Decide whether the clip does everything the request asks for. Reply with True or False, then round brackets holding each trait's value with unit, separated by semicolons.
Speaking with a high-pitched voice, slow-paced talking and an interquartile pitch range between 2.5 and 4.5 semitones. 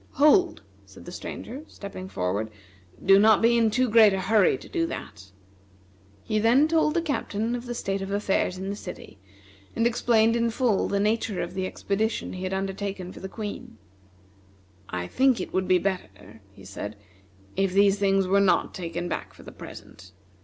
False (200 Hz; 185 wpm; 3.7 semitones)